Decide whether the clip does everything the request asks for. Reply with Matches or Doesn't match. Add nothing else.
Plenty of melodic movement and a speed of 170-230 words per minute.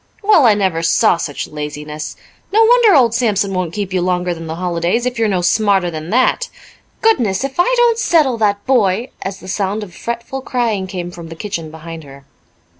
Matches